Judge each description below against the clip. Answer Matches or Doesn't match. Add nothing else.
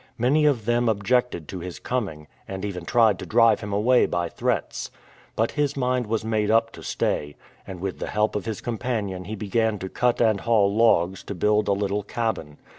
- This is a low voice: Matches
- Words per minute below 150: Doesn't match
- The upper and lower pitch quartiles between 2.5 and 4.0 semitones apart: Matches